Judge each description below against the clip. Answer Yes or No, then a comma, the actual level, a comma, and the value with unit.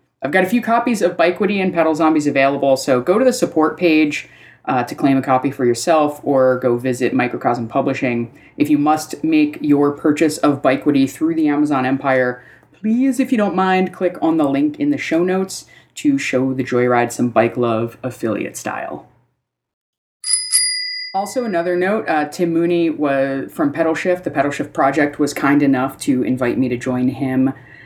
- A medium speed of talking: Yes, average, 185 wpm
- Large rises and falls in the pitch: Yes, wide, 5.9 semitones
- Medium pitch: Yes, medium, 150 Hz